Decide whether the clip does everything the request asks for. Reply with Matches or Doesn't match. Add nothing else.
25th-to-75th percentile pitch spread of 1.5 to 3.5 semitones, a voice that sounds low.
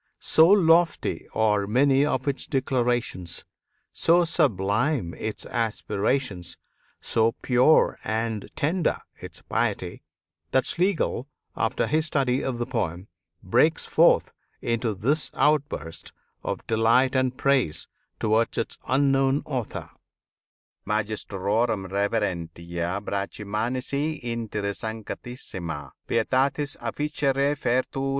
Doesn't match